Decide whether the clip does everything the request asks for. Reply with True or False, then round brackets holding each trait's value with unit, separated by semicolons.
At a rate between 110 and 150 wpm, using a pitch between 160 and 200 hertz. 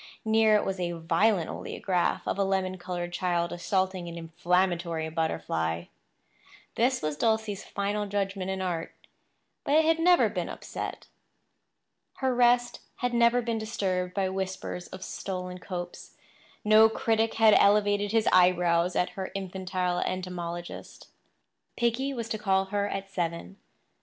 True (140 wpm; 190 Hz)